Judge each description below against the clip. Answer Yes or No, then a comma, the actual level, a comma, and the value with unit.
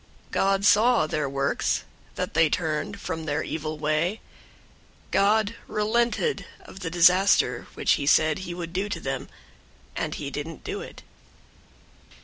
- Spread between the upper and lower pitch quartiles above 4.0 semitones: Yes, average, 4.9 semitones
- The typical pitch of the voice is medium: Yes, medium, 175 Hz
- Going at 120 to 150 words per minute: Yes, average, 145 wpm